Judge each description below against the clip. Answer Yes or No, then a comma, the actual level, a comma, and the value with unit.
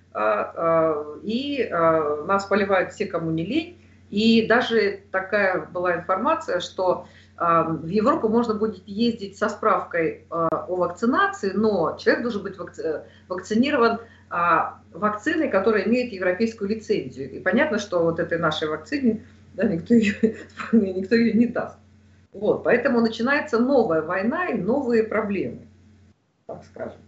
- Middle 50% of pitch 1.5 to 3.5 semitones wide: No, average, 5.0 semitones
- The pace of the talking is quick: No, average, 125 wpm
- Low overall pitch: No, high, 210 Hz